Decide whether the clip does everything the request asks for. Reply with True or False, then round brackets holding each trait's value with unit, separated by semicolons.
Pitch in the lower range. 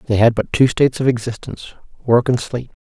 True (120 Hz)